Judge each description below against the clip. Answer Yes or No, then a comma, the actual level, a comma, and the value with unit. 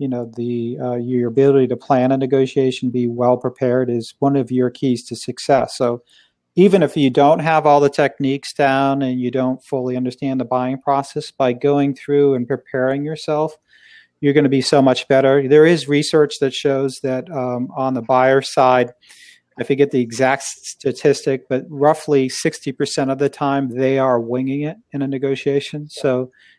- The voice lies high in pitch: No, low, 135 Hz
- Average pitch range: No, narrow, 1.9 semitones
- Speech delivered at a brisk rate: No, average, 185 wpm